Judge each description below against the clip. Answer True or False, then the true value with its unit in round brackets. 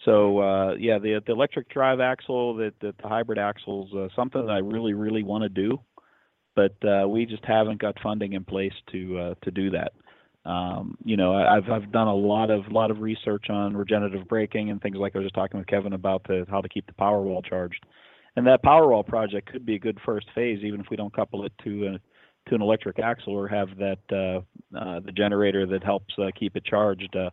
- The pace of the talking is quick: True (235 wpm)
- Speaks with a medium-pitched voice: False (100 Hz)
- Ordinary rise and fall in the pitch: False (2.0 semitones)